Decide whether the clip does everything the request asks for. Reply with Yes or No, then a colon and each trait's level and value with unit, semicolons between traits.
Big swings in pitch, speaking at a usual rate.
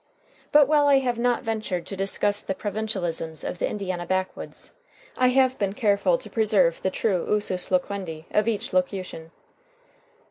No: average, 3.5 semitones; average, 155 wpm